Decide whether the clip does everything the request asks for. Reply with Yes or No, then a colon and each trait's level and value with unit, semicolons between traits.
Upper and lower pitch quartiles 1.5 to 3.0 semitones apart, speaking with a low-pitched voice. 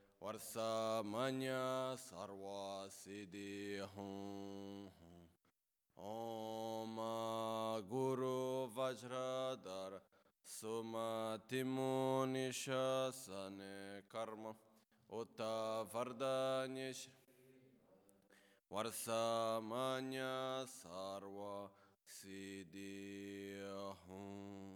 No: average, 4.6 semitones; low, 110 Hz